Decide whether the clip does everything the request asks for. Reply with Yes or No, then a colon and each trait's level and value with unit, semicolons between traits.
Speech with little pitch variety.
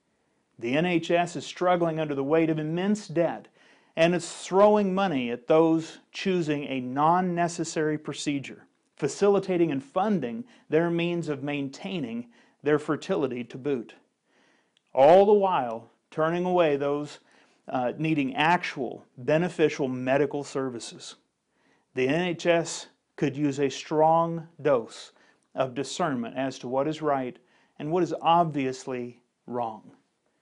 No: average, 3.8 semitones